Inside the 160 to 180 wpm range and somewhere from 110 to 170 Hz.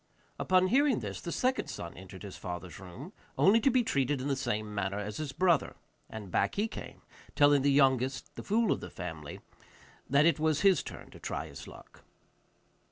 No: average, 195 wpm; medium, 140 Hz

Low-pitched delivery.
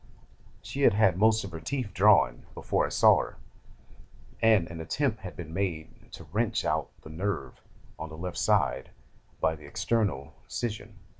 Yes: very low, 95 Hz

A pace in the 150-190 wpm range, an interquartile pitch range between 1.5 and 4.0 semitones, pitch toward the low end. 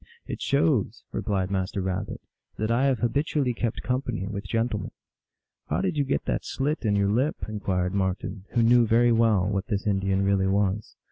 No: average, 200 wpm; average, 3.7 semitones; low, 105 Hz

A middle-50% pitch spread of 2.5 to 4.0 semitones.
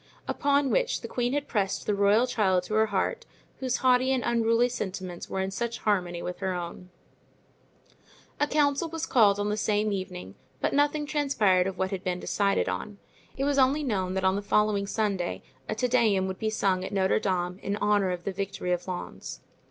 No: average, 4.7 semitones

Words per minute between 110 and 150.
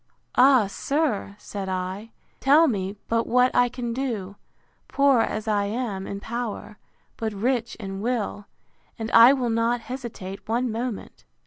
Yes: average, 145 wpm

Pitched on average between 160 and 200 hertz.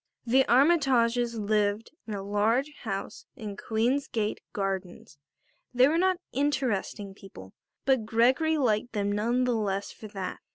No: high, 225 Hz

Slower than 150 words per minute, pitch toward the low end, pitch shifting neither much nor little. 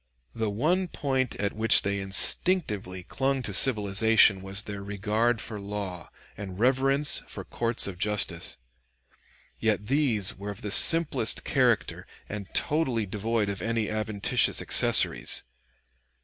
Yes: slow, 135 wpm; low, 105 Hz; average, 3.6 semitones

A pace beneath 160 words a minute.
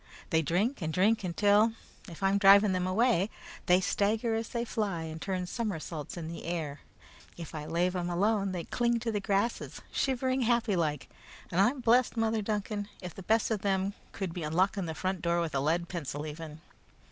No: average, 195 wpm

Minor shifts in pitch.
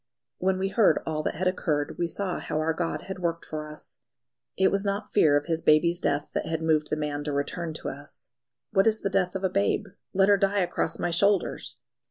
No: average, 3.9 semitones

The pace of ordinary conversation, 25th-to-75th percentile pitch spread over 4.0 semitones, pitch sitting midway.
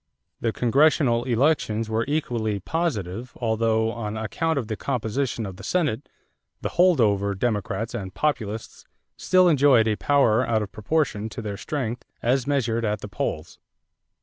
No: average, 150 wpm; average, 4.4 semitones; low, 115 Hz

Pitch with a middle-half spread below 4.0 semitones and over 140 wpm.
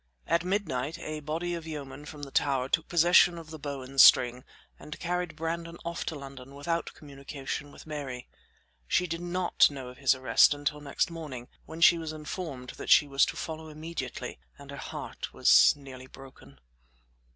Yes: average, 3.5 semitones; average, 180 wpm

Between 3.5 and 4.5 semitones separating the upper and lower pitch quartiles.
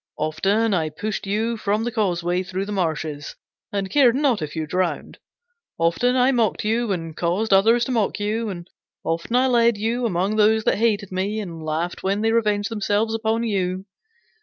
Yes: average, 4.0 semitones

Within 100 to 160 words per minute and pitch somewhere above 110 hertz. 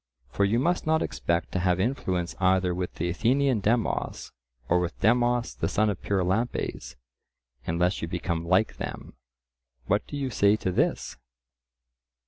No: average, 150 wpm; very low, 95 Hz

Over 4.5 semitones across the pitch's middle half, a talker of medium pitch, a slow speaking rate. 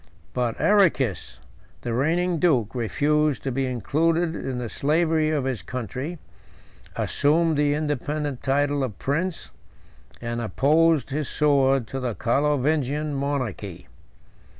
No: average, 3.4 semitones; medium, 145 Hz; slow, 120 wpm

